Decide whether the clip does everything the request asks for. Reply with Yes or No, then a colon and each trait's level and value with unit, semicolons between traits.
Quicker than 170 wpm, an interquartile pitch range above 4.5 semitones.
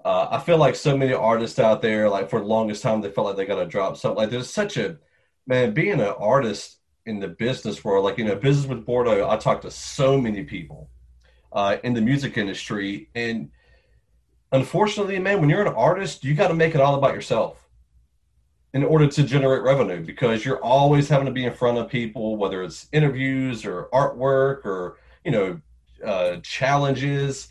Yes: average, 200 wpm; wide, 5.5 semitones